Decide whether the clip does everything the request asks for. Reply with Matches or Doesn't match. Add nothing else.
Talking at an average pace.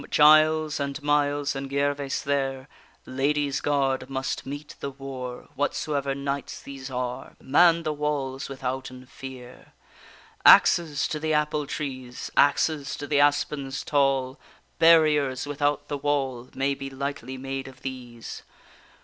Doesn't match